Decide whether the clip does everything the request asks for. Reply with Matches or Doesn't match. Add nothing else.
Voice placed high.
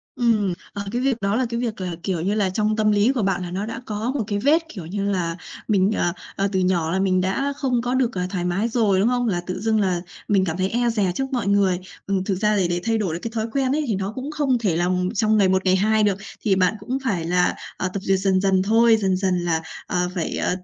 Matches